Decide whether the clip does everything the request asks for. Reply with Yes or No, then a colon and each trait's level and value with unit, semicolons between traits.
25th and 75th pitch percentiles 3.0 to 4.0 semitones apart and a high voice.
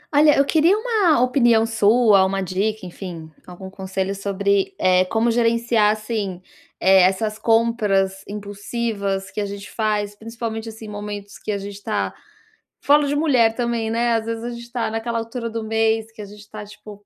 No: narrow, 2.6 semitones; high, 220 Hz